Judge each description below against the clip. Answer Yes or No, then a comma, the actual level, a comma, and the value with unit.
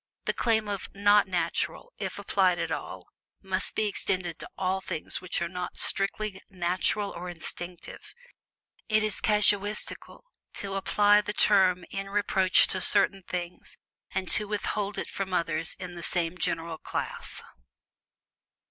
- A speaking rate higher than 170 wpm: No, average, 145 wpm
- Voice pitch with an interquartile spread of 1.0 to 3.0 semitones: Yes, narrow, 2.5 semitones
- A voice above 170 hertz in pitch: Yes, high, 190 Hz